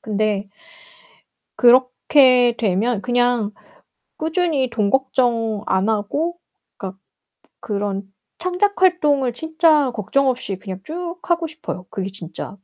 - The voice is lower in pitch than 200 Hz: No, high, 245 Hz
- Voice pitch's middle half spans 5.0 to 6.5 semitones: No, wide, 6.9 semitones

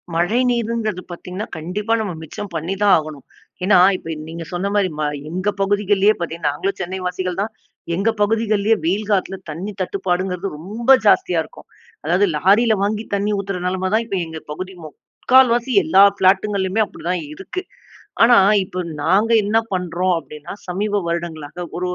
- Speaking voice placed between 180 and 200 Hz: Yes, high, 190 Hz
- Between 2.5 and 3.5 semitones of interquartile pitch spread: Yes, average, 2.9 semitones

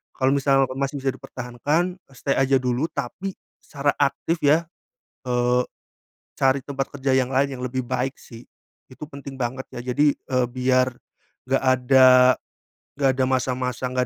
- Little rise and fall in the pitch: Yes, narrow, 1.5 semitones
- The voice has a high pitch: No, low, 130 Hz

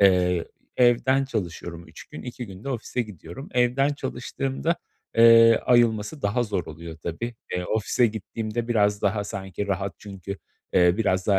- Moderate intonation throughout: Yes, average, 4.5 semitones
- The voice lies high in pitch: No, low, 105 Hz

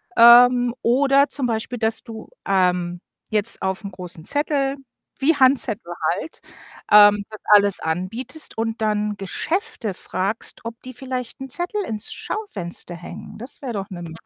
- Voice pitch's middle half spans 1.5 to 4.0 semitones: No, average, 4.9 semitones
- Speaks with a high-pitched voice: Yes, high, 225 Hz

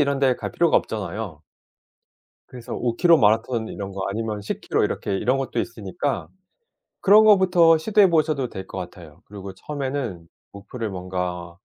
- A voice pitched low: Yes, low, 115 Hz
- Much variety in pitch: Yes, wide, 6.9 semitones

